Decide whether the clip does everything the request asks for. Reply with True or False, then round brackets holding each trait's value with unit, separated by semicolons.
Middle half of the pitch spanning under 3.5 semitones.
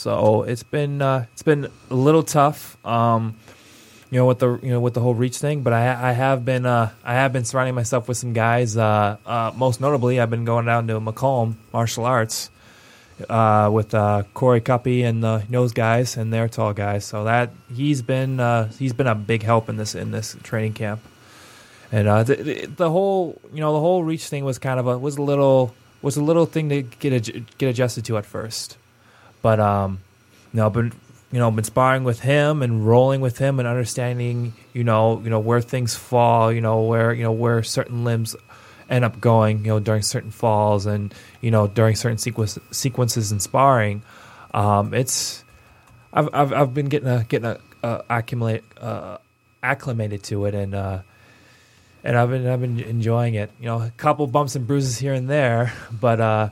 True (2.7 semitones)